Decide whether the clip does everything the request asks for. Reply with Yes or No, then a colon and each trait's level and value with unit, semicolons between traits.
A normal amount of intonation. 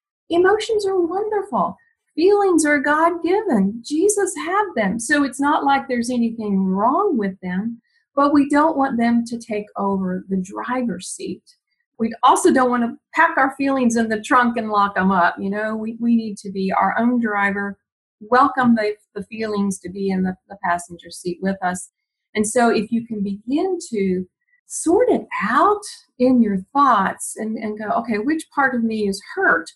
No: wide, 7.7 semitones